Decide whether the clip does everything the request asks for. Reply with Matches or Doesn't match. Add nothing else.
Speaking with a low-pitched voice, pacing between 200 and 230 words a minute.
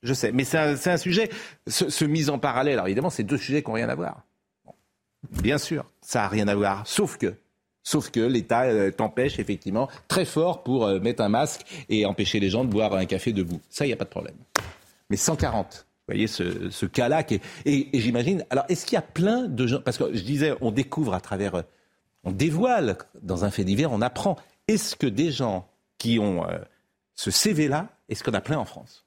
Matches